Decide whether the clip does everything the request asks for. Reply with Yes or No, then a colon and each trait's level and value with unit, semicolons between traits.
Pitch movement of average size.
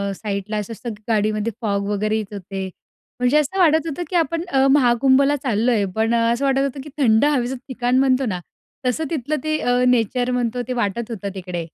Yes: average, 4.1 semitones